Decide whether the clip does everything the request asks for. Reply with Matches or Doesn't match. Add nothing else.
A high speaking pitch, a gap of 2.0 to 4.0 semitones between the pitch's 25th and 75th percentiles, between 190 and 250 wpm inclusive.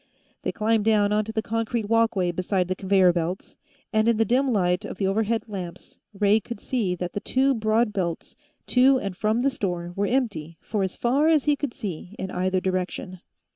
Matches